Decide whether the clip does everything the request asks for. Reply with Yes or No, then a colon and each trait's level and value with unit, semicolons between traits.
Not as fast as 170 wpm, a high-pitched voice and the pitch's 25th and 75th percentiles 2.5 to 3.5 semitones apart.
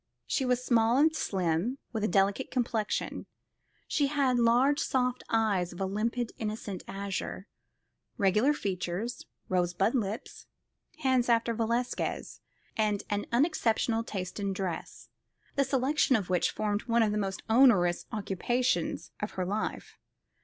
No: slow, 135 wpm; high, 220 Hz; average, 4.2 semitones